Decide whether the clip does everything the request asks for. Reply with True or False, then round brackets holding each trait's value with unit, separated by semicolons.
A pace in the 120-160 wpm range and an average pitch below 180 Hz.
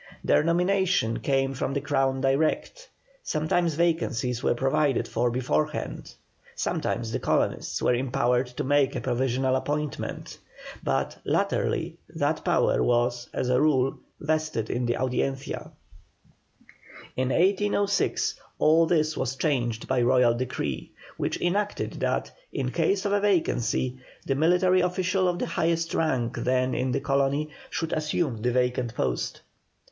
True (135 wpm; 135 Hz)